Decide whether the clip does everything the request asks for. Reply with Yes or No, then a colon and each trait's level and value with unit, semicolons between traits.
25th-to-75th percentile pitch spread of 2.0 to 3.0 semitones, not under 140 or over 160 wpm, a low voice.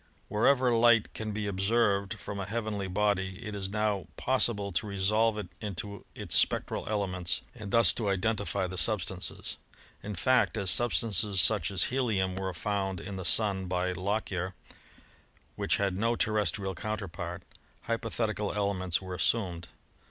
Yes: narrow, 2.4 semitones; average, 155 wpm; low, 100 Hz